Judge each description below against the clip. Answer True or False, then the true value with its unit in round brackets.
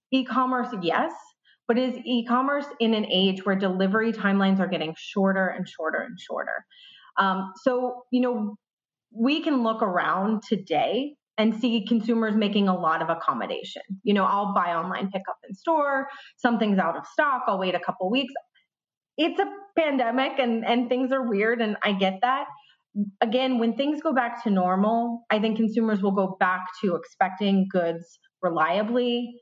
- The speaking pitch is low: False (220 Hz)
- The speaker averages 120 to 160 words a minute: False (170 wpm)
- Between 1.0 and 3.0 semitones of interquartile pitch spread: False (4.8 semitones)